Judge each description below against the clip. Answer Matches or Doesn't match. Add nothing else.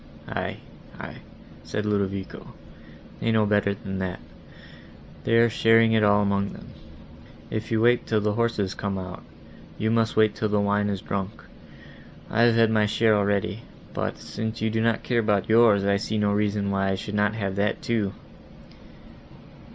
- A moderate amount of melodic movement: Doesn't match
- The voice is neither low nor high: Doesn't match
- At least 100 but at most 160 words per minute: Doesn't match